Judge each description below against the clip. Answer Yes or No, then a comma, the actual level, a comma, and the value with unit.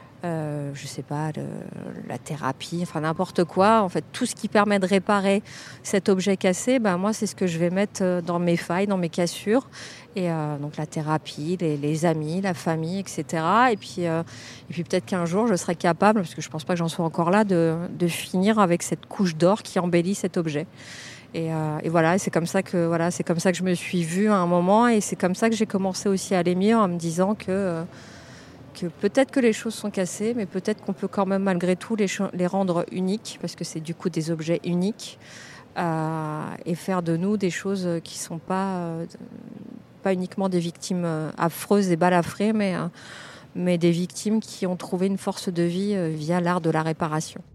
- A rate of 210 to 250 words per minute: Yes, fast, 220 wpm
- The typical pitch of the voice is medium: Yes, medium, 180 Hz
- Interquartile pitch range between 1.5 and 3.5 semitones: Yes, average, 3.0 semitones